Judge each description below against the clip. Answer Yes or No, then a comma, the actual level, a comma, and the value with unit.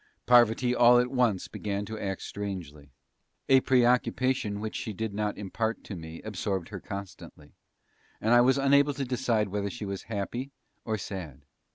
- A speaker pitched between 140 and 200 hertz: No, low, 110 Hz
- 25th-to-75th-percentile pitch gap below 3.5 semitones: No, average, 3.8 semitones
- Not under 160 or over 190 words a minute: Yes, average, 165 wpm